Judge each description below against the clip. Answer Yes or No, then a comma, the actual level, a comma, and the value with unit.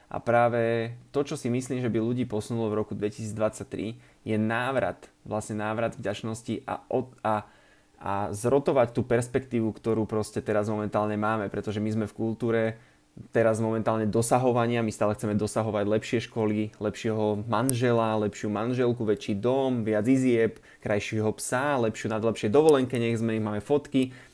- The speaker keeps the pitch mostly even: Yes, narrow, 2.0 semitones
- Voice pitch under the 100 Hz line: No, low, 110 Hz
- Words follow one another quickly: No, average, 155 wpm